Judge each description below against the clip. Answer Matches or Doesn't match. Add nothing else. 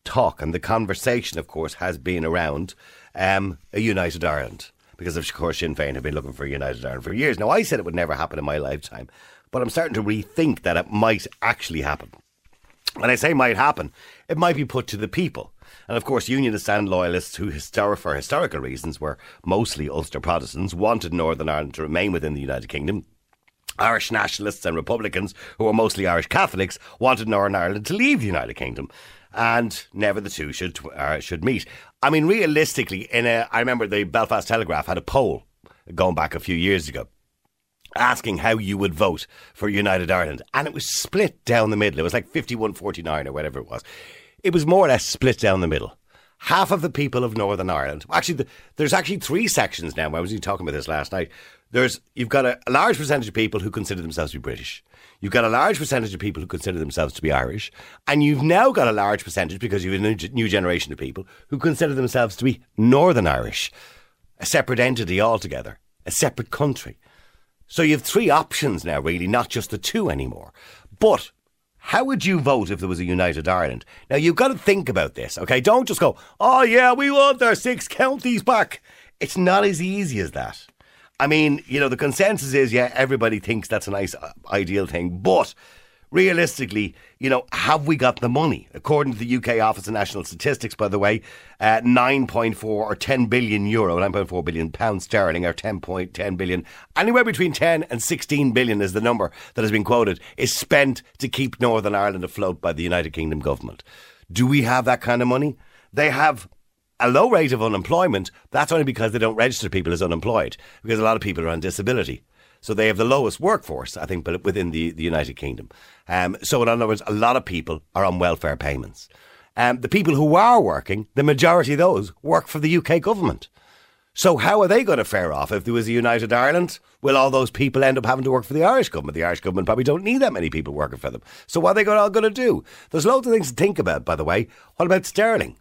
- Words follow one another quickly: Matches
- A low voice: Matches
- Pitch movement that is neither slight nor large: Doesn't match